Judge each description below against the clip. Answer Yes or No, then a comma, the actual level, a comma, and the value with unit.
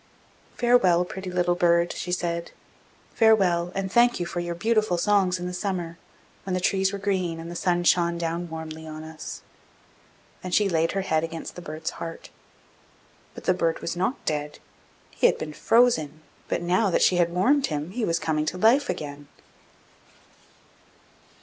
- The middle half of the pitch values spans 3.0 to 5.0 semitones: No, narrow, 2.6 semitones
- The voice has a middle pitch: Yes, medium, 175 Hz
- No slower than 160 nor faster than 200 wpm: Yes, average, 175 wpm